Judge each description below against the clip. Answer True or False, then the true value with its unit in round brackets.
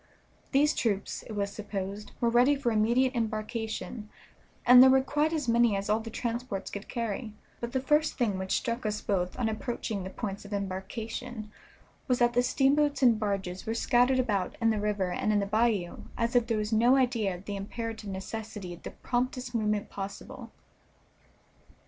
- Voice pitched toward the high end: True (225 Hz)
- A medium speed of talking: True (185 wpm)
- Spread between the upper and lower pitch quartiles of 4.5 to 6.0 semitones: False (3.3 semitones)